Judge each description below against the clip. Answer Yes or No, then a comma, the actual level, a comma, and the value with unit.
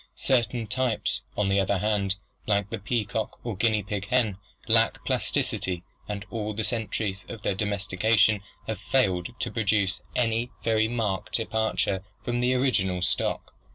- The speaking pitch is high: No, low, 110 Hz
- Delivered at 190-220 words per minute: No, average, 145 wpm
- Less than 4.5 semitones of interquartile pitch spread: Yes, average, 2.8 semitones